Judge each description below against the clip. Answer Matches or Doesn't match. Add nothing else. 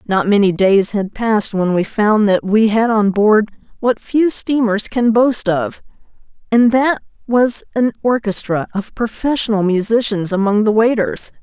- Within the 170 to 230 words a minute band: Doesn't match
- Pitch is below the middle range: Doesn't match